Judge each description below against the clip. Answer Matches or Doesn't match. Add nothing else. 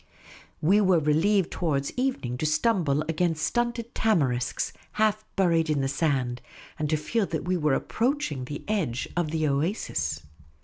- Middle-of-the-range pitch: Matches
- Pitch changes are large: Matches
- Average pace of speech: Matches